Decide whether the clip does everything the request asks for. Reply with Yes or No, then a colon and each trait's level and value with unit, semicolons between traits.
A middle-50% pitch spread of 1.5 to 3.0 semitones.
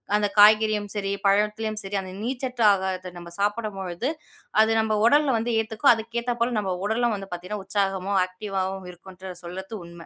Yes: average, 2.7 semitones